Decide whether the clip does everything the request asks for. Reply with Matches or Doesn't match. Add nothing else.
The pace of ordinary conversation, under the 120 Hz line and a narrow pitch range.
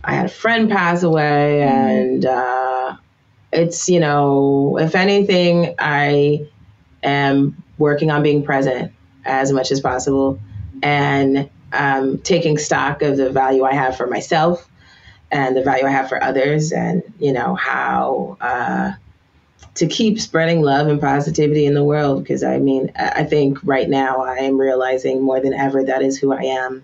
Doesn't match